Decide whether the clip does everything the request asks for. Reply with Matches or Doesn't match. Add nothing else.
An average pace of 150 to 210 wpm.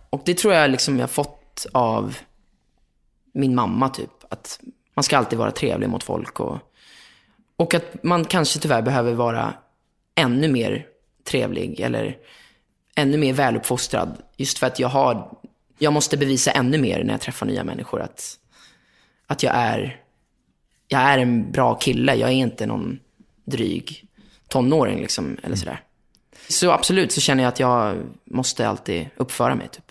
Matches